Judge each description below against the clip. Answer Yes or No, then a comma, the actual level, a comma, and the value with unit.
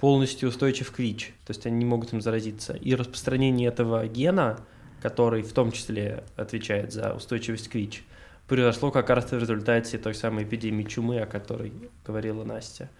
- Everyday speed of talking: No, fast, 170 wpm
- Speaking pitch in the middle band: No, low, 115 Hz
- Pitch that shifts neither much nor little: No, narrow, 2.2 semitones